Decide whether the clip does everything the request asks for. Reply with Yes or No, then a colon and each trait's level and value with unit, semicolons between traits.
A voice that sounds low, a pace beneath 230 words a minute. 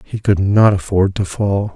Yes: low, 100 Hz; fast, 205 wpm